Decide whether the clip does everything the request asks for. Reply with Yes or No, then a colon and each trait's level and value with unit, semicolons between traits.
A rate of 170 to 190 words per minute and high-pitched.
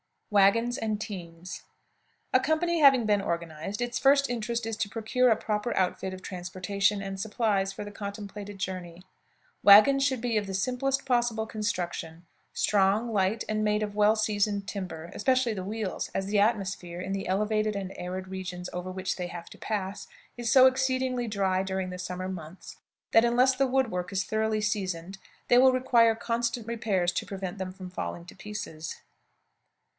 Yes: average, 175 wpm; high, 205 Hz